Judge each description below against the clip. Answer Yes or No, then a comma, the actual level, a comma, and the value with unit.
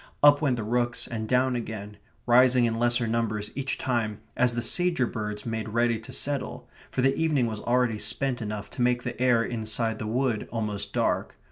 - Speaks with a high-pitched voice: No, low, 120 Hz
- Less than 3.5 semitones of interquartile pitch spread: Yes, narrow, 2.5 semitones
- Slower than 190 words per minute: No, average, 195 wpm